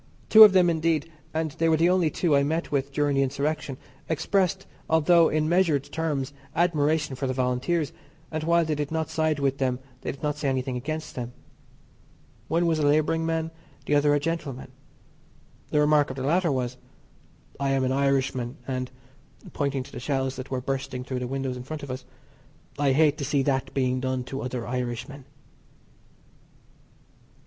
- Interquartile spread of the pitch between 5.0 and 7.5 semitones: No, average, 3.3 semitones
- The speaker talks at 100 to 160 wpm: No, average, 185 wpm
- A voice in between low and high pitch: Yes, medium, 145 Hz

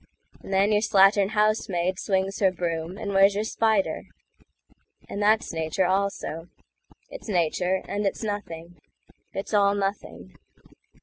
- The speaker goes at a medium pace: No, slow, 120 wpm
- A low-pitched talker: No, high, 195 Hz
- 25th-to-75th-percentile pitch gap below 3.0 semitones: Yes, narrow, 2.5 semitones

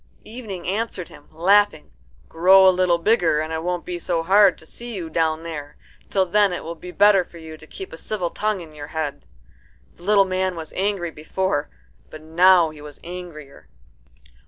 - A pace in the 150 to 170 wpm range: No, average, 190 wpm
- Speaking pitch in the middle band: Yes, medium, 175 Hz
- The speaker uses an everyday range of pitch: Yes, average, 3.2 semitones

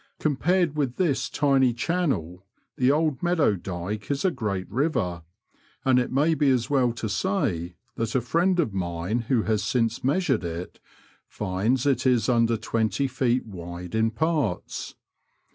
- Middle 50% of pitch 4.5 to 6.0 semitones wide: Yes, wide, 5.6 semitones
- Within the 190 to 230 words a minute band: No, average, 155 wpm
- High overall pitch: No, low, 120 Hz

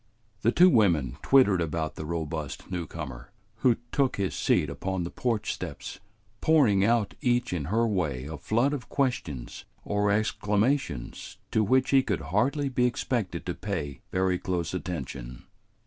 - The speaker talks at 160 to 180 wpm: No, average, 150 wpm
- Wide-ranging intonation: Yes, wide, 7.1 semitones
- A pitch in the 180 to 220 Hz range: No, very low, 95 Hz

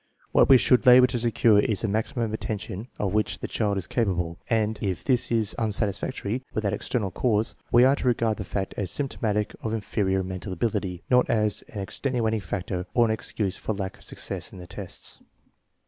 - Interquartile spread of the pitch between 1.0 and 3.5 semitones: Yes, average, 3.2 semitones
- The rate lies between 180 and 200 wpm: Yes, average, 195 wpm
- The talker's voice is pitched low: Yes, low, 105 Hz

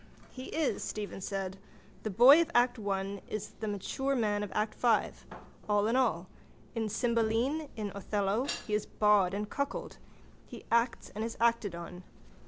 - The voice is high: Yes, high, 215 Hz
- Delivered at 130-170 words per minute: Yes, average, 165 wpm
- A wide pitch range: No, average, 3.0 semitones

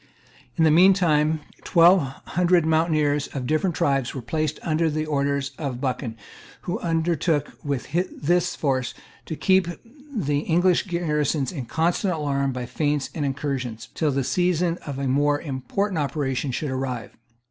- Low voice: No, medium, 150 Hz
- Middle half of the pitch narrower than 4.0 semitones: Yes, average, 3.4 semitones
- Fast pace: No, average, 145 wpm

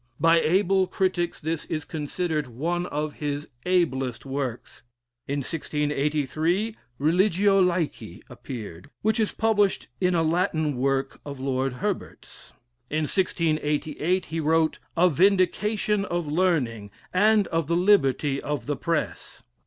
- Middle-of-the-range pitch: Yes, medium, 160 Hz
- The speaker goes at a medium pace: No, slow, 125 wpm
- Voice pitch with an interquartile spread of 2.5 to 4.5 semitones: Yes, average, 4.2 semitones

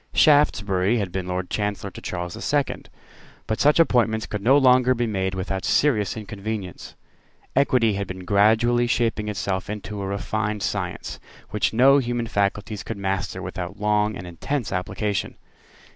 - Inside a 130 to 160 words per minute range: Yes, average, 155 wpm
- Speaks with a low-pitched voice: Yes, low, 105 Hz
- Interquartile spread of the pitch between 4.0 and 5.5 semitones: No, average, 3.6 semitones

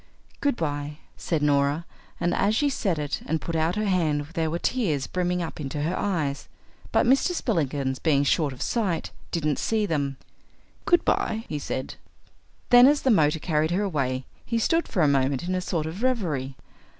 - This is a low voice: No, medium, 160 Hz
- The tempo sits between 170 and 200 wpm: Yes, average, 180 wpm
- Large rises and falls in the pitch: Yes, wide, 5.7 semitones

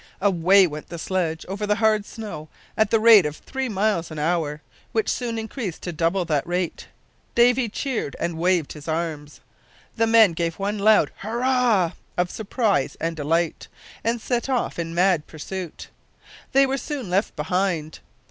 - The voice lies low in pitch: No, high, 190 Hz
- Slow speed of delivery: No, average, 165 wpm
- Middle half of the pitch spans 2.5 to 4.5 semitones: No, average, 5.2 semitones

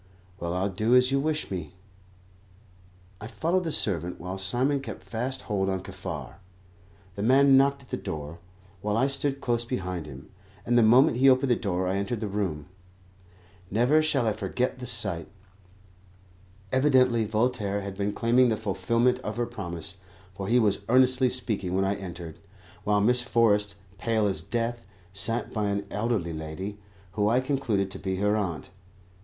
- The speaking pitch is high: No, low, 110 Hz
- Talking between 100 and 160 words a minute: No, average, 170 wpm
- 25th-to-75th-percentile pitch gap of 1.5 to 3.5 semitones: No, average, 4.5 semitones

